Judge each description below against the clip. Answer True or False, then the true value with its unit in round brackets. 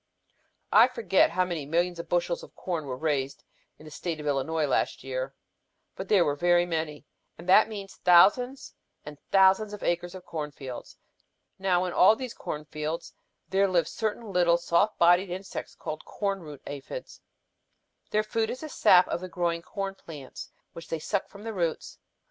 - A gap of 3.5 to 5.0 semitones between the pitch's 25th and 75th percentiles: True (4.0 semitones)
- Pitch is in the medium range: True (175 Hz)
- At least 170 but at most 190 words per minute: True (180 wpm)